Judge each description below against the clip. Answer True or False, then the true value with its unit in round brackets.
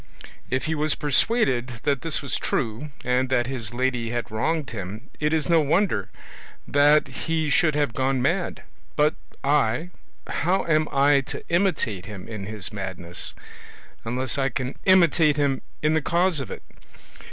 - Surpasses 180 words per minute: False (160 wpm)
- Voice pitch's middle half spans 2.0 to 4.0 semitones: False (4.4 semitones)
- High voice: False (140 Hz)